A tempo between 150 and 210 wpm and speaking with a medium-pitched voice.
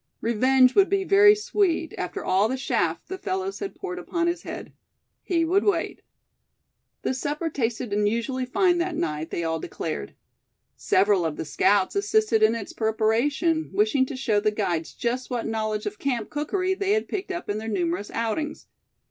No: average, 175 wpm; very high, 260 Hz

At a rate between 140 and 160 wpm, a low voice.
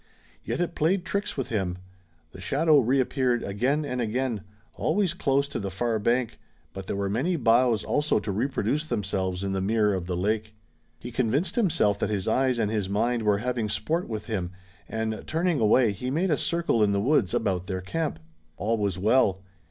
No: average, 195 wpm; low, 115 Hz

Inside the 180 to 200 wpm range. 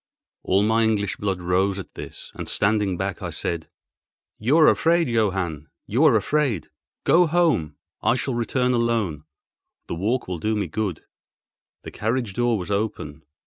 No: average, 155 wpm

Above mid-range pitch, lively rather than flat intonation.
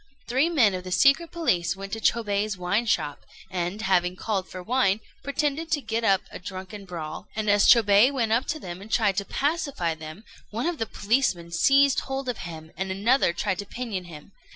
Yes: high, 205 Hz; wide, 5.7 semitones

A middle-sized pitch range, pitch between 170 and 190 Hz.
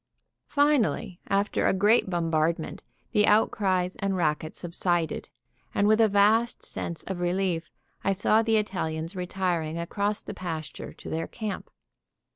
Yes: average, 3.6 semitones; medium, 185 Hz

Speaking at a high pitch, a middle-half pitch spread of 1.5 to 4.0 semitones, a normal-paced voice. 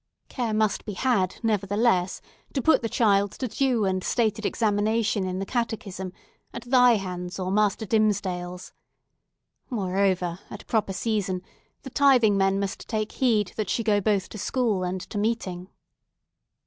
Yes: high, 205 Hz; average, 3.2 semitones; average, 155 wpm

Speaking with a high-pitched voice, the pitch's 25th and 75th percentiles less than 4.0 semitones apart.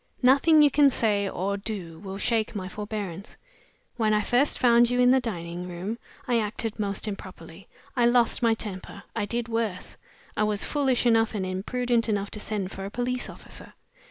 Yes: high, 215 Hz; average, 3.4 semitones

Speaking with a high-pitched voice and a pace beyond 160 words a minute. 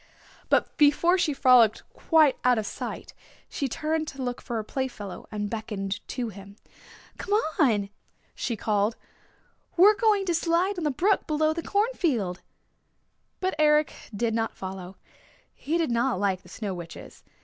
No: very high, 255 Hz; average, 155 wpm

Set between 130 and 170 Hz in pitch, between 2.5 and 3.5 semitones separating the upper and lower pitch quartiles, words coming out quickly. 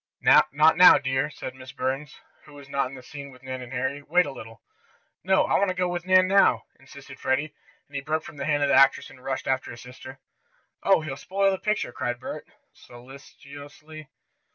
Yes: medium, 140 Hz; average, 3.1 semitones; fast, 210 wpm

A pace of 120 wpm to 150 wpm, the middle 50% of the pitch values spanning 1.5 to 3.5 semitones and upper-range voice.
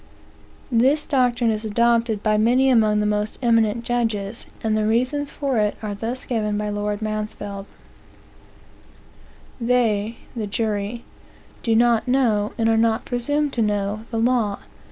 Yes: average, 145 wpm; narrow, 2.4 semitones; high, 225 Hz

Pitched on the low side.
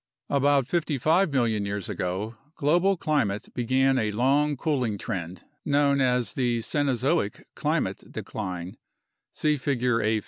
Yes: low, 125 Hz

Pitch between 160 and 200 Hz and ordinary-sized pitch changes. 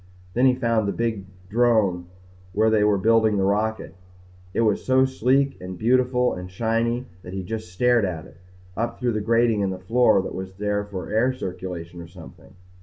No: low, 110 Hz; average, 4.0 semitones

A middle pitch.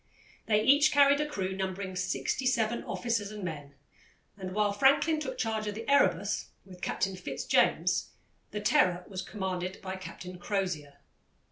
No: high, 200 Hz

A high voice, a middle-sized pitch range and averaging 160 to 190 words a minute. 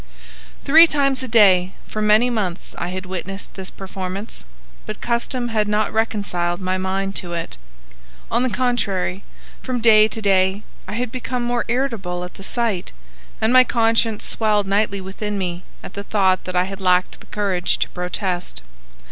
Yes: high, 200 Hz; average, 3.5 semitones; average, 170 wpm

